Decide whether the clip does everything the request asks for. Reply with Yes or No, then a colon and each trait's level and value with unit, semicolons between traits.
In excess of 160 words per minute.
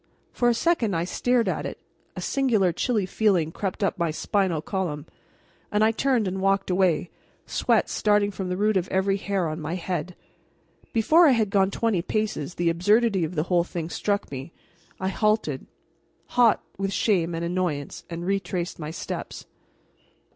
Yes: average, 170 wpm